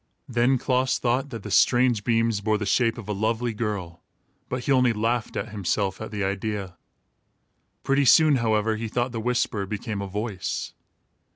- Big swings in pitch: No, average, 3.0 semitones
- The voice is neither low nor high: No, low, 115 Hz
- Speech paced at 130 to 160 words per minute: No, average, 175 wpm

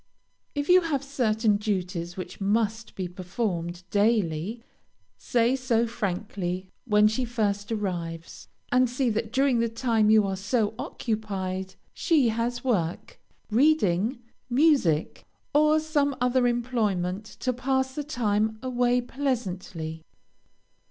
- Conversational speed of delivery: No, slow, 120 wpm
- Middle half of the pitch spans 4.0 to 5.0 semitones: Yes, average, 4.7 semitones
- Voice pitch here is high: Yes, high, 225 Hz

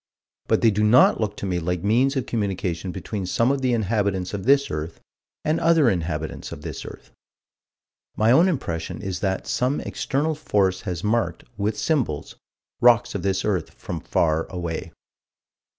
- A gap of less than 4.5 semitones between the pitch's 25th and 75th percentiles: No, average, 5.1 semitones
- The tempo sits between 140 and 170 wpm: Yes, average, 165 wpm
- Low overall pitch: Yes, low, 105 Hz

